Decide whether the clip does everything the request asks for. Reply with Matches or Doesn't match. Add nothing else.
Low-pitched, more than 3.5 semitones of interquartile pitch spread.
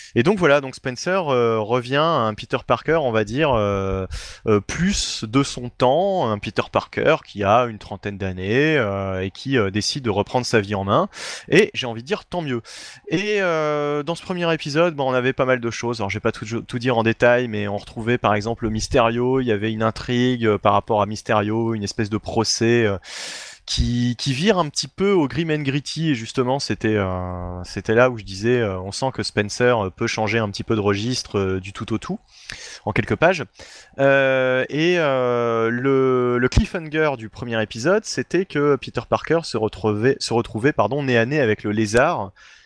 Matches